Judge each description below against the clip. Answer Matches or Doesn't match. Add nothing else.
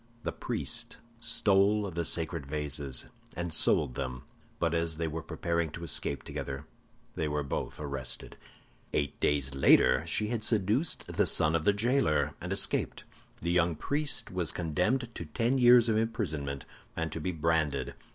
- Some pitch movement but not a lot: Doesn't match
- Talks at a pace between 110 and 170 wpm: Matches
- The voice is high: Doesn't match